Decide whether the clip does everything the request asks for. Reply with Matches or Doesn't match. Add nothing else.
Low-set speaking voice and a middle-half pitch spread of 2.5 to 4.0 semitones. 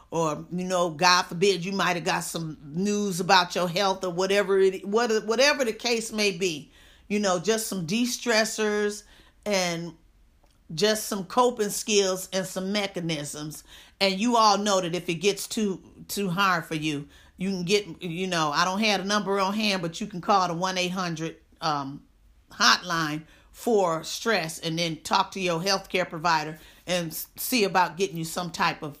Doesn't match